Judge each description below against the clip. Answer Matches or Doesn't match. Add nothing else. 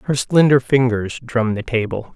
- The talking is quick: Doesn't match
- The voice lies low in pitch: Matches